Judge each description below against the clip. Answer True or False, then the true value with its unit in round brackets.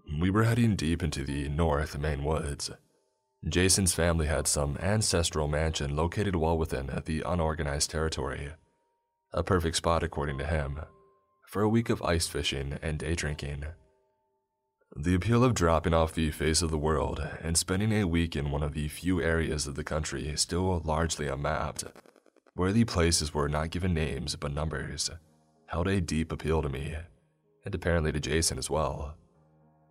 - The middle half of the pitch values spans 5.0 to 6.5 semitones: False (3.1 semitones)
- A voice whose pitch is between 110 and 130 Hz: False (80 Hz)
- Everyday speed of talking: True (165 wpm)